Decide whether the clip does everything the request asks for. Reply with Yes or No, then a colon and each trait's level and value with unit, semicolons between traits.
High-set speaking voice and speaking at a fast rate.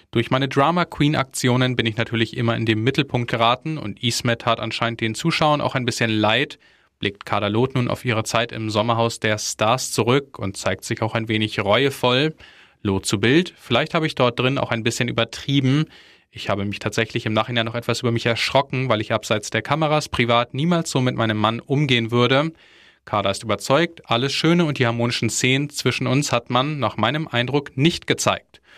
No: low, 120 Hz; fast, 200 wpm